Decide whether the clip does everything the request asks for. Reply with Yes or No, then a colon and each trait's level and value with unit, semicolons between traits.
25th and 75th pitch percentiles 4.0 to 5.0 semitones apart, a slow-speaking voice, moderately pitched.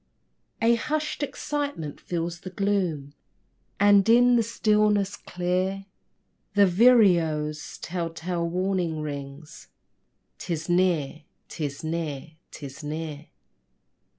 Yes: average, 4.6 semitones; slow, 95 wpm; medium, 175 Hz